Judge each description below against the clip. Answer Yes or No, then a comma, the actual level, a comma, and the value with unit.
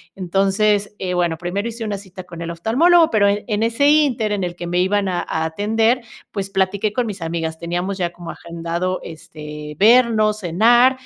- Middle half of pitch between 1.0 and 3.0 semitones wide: No, average, 4.1 semitones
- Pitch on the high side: Yes, high, 195 Hz